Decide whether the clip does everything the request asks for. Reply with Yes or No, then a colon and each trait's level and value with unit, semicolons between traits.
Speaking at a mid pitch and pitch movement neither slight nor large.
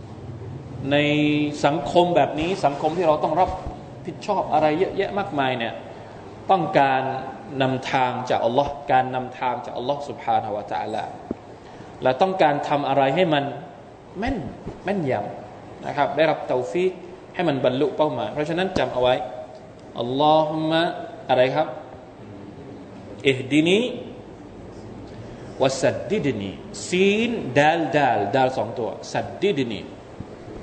Yes: medium, 145 Hz; average, 3.5 semitones